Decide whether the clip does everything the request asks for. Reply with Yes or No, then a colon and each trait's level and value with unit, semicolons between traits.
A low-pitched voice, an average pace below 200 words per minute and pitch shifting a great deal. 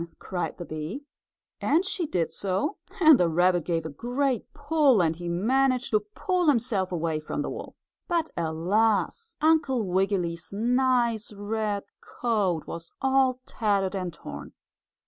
No: high, 210 Hz; average, 145 wpm; wide, 7.1 semitones